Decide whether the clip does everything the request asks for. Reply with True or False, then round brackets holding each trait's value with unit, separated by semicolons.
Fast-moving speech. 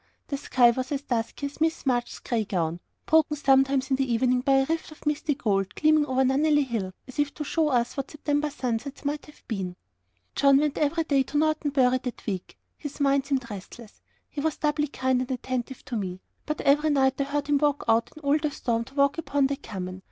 True (220 wpm)